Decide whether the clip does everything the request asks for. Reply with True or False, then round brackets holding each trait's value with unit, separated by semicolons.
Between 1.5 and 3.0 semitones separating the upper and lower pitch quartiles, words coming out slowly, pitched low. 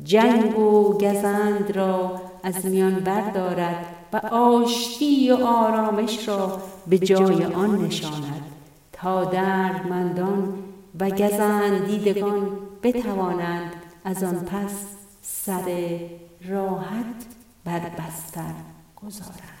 False (2.4 semitones; 90 wpm; 190 Hz)